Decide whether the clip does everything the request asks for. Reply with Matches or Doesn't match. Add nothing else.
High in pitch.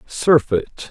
Doesn't match